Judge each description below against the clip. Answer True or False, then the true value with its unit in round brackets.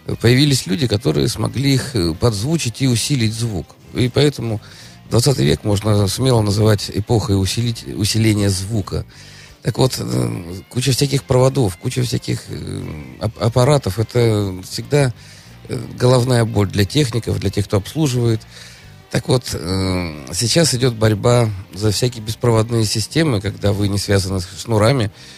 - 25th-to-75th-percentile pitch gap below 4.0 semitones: False (4.3 semitones)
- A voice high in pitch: False (110 Hz)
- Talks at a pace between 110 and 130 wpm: True (125 wpm)